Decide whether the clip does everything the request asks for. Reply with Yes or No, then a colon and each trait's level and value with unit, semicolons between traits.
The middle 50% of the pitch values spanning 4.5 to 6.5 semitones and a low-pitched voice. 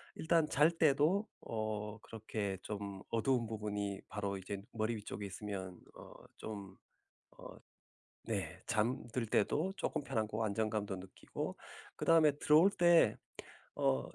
Yes: average, 5.2 semitones; low, 110 Hz